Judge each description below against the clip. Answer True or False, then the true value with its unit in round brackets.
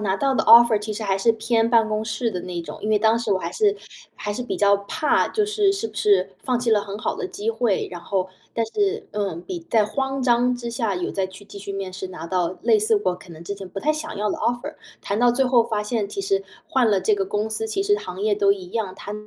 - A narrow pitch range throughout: False (3.7 semitones)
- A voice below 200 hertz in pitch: False (215 Hz)